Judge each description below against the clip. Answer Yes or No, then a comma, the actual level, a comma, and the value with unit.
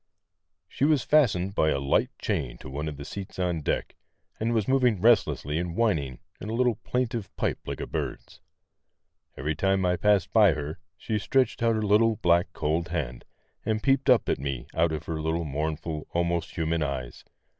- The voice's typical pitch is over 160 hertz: No, very low, 85 Hz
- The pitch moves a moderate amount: No, wide, 6.1 semitones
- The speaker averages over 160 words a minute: Yes, average, 190 wpm